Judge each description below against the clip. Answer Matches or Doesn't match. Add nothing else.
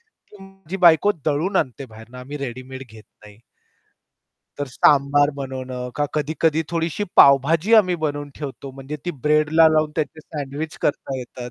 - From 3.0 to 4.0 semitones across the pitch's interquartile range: Matches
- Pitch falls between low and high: Matches